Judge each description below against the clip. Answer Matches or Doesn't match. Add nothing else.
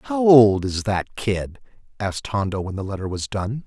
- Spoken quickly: Doesn't match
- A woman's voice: Doesn't match